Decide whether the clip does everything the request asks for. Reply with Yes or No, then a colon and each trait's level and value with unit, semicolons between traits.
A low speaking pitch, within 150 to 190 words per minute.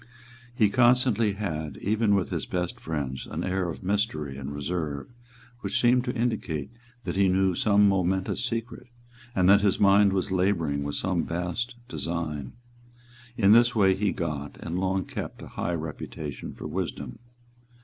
Yes: very low, 95 Hz; average, 160 wpm